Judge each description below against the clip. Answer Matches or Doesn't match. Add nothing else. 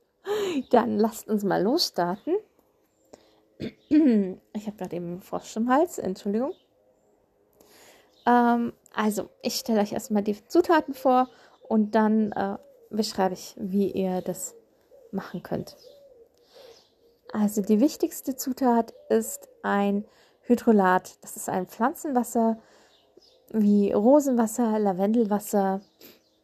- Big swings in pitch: Matches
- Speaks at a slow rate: Matches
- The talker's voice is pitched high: Matches